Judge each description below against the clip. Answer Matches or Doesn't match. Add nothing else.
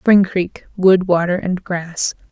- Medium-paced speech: Doesn't match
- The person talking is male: Doesn't match